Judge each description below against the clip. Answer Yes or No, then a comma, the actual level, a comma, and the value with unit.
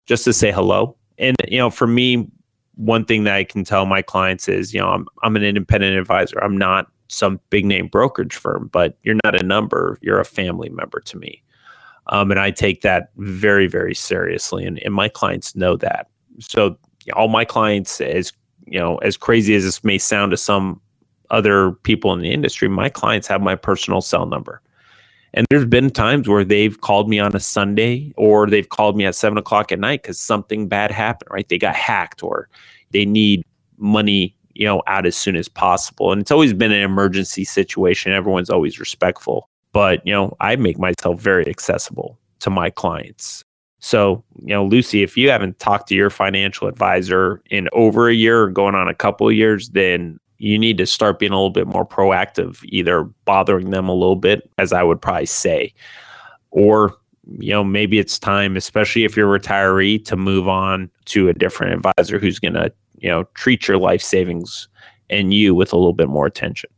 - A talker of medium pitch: No, low, 100 Hz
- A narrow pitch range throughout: Yes, narrow, 2.0 semitones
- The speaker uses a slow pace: No, average, 200 wpm